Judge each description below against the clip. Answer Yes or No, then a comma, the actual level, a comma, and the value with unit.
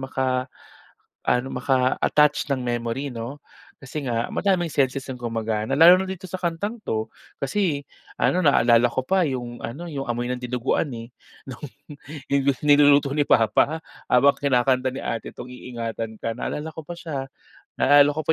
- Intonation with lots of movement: No, average, 3.6 semitones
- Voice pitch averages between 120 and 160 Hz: Yes, low, 135 Hz